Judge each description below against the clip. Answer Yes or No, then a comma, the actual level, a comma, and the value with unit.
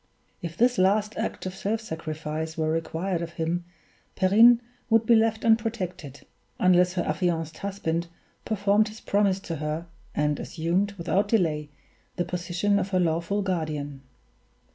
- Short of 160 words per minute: Yes, average, 140 wpm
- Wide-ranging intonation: No, average, 4.0 semitones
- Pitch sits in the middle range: Yes, medium, 180 Hz